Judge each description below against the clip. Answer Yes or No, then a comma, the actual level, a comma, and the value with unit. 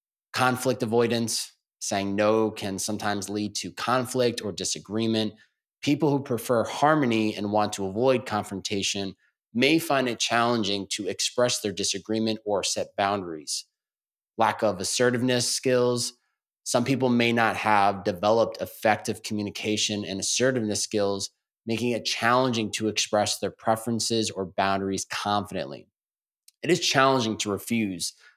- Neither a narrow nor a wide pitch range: Yes, average, 3.1 semitones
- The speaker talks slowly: Yes, slow, 130 wpm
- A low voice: Yes, low, 110 Hz